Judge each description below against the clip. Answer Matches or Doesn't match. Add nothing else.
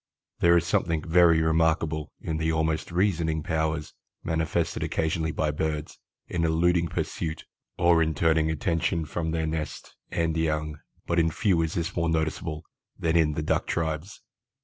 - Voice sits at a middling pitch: Doesn't match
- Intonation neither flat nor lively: Doesn't match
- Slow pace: Doesn't match